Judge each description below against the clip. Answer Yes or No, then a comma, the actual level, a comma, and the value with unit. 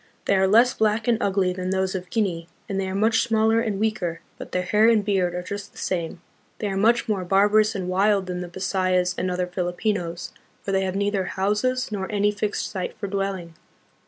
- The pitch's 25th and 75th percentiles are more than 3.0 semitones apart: No, narrow, 2.6 semitones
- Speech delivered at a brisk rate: Yes, fast, 215 wpm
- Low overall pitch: No, high, 195 Hz